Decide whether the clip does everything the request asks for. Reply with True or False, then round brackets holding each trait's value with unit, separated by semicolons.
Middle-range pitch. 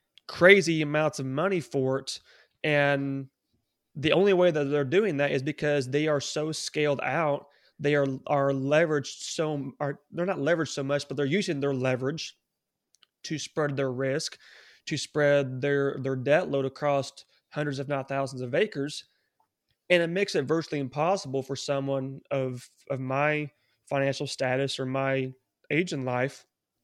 True (145 Hz)